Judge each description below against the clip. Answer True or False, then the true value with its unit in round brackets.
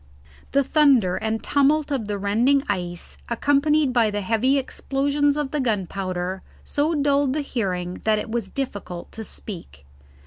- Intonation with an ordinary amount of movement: False (5.9 semitones)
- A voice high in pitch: True (235 Hz)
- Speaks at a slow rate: False (150 wpm)